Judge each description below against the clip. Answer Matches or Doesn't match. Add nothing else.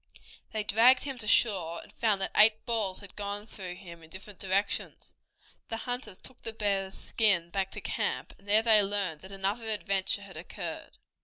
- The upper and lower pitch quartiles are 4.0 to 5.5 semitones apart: Doesn't match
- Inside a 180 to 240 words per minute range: Matches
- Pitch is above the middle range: Matches